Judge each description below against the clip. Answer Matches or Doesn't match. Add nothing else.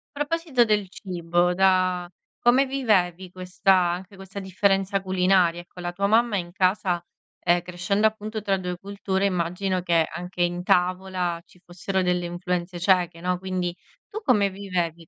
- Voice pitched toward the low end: Doesn't match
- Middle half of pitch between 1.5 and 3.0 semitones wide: Matches